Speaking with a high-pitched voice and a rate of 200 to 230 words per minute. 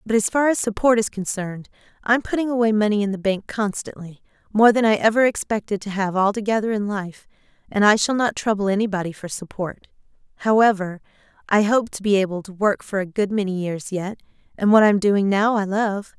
Yes: high, 205 Hz; fast, 205 wpm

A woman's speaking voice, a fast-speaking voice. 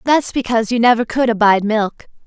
No: female; average, 185 wpm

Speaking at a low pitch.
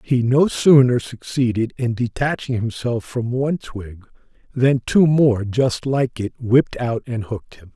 Yes: low, 120 Hz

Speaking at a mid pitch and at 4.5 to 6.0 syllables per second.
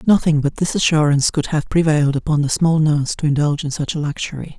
No: medium, 150 Hz; 6.5 syllables/s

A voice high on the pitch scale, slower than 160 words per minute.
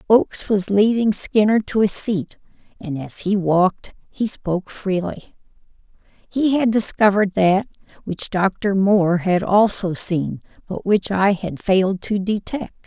Yes: high, 195 Hz; average, 145 wpm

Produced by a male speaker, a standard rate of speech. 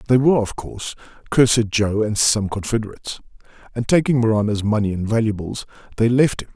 Yes: male; average, 165 wpm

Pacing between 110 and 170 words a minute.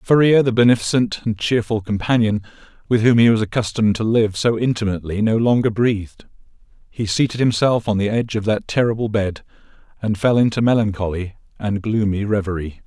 Yes: average, 165 wpm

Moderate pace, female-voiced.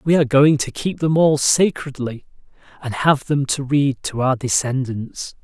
No: average, 175 wpm; male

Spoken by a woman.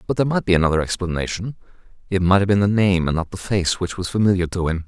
No: male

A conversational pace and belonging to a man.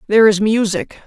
No: average, 170 wpm; female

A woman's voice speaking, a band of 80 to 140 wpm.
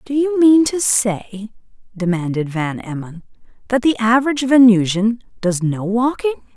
Yes: female; slow, 135 wpm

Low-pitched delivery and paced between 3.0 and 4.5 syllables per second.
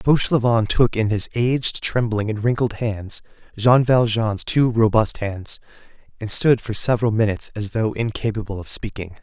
No: low, 110 Hz; 4.9 syllables/s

